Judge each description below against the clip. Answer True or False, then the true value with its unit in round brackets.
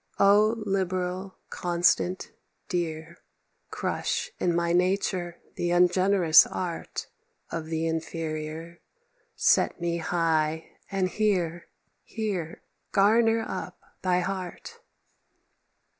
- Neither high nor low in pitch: True (175 Hz)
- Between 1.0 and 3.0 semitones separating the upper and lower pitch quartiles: True (2.4 semitones)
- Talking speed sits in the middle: False (90 wpm)